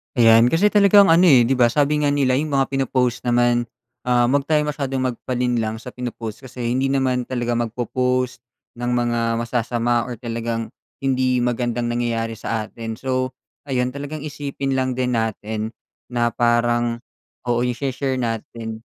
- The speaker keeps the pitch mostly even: Yes, narrow, 2.1 semitones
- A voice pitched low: Yes, low, 125 Hz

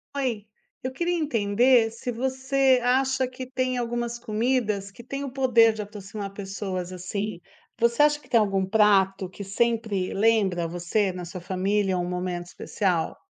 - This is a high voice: Yes, high, 215 Hz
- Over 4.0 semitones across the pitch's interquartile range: Yes, average, 4.7 semitones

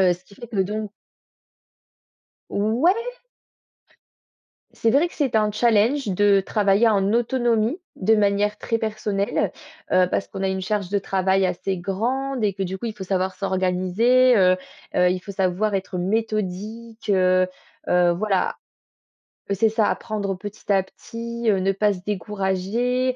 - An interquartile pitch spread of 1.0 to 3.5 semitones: Yes, average, 2.9 semitones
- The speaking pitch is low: No, high, 205 Hz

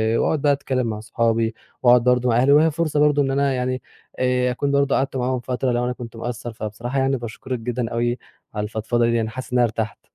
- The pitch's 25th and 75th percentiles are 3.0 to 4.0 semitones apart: No, narrow, 2.4 semitones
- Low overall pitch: Yes, low, 125 Hz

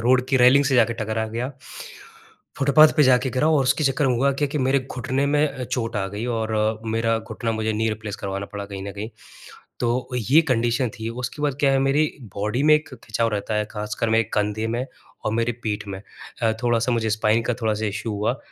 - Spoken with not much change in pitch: No, average, 3.4 semitones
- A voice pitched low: Yes, low, 115 Hz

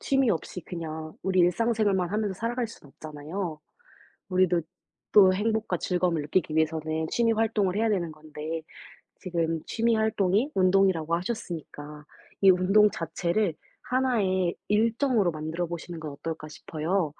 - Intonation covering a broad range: No, average, 4.8 semitones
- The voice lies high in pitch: No, medium, 180 Hz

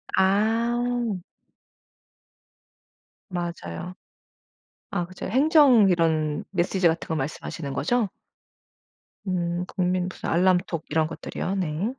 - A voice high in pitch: No, medium, 180 Hz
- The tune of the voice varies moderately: Yes, average, 4.0 semitones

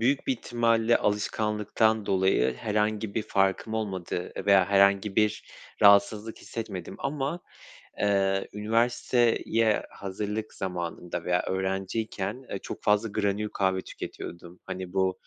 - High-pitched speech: No, low, 105 Hz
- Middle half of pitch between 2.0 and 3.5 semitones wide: Yes, narrow, 2.5 semitones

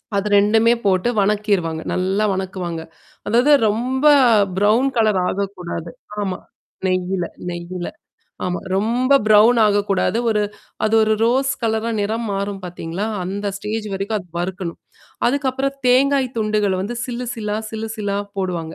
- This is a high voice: Yes, high, 205 Hz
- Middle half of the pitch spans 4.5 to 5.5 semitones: No, average, 3.3 semitones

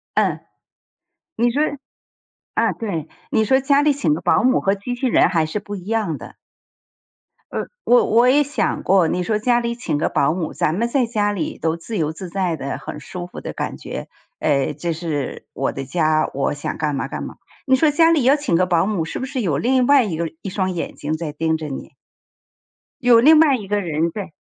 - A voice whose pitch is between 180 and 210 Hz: Yes, high, 195 Hz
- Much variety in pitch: Yes, wide, 7.2 semitones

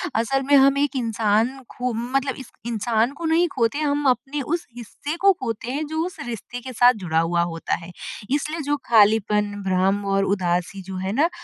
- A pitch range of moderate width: No, wide, 5.7 semitones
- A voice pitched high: Yes, high, 235 Hz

